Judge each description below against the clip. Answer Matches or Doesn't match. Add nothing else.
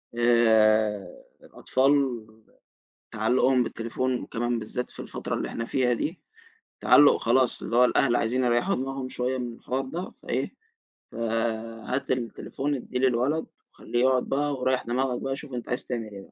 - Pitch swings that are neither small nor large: Doesn't match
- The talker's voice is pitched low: Matches